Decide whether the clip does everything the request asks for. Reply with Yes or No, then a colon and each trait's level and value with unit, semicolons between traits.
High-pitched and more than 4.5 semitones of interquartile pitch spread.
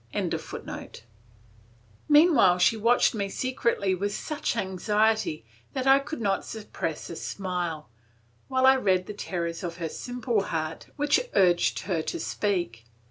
Yes: high, 200 Hz; wide, 5.6 semitones